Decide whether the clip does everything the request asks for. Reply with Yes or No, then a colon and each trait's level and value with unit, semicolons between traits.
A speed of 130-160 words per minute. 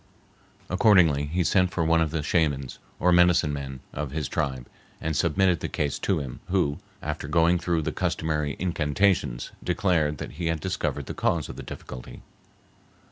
No: average, 170 wpm